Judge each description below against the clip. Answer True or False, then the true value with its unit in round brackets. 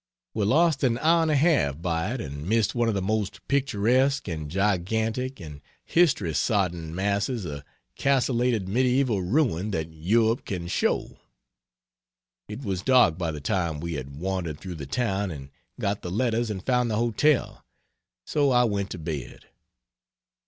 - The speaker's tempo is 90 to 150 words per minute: False (160 wpm)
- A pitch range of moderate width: False (6.4 semitones)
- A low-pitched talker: True (100 Hz)